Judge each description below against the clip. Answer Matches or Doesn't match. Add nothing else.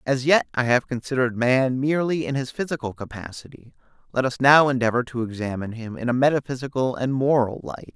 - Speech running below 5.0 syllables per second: Doesn't match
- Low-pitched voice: Matches